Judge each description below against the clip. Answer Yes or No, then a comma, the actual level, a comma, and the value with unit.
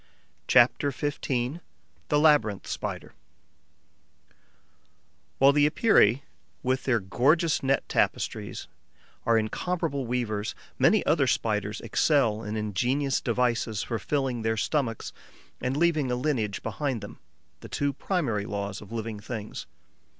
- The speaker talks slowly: Yes, slow, 120 wpm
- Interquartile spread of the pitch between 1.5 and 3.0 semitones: No, average, 4.7 semitones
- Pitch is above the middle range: No, low, 125 Hz